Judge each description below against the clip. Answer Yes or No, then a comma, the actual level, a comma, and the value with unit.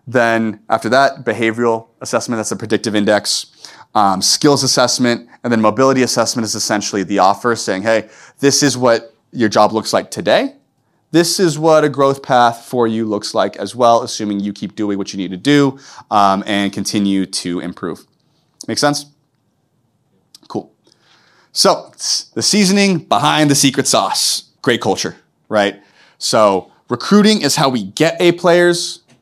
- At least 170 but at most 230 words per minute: No, average, 160 wpm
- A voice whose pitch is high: No, low, 115 Hz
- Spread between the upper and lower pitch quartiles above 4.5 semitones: Yes, average, 5.1 semitones